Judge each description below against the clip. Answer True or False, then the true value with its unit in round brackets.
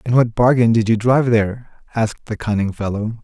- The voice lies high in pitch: False (115 Hz)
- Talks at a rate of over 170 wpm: True (205 wpm)